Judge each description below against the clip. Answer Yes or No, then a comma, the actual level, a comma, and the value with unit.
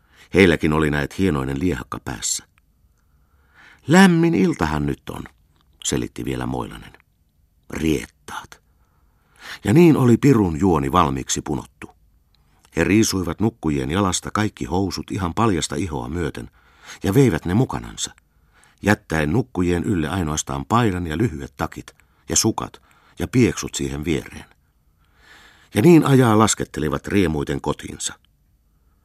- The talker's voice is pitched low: Yes, very low, 80 Hz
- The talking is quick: No, average, 115 wpm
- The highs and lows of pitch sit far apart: Yes, wide, 6.6 semitones